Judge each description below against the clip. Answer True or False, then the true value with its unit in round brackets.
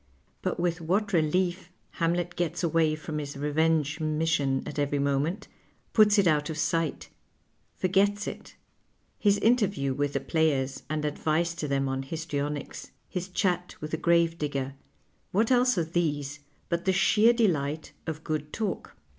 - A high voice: False (160 Hz)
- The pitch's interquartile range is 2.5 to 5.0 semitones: True (3.3 semitones)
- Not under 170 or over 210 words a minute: False (155 wpm)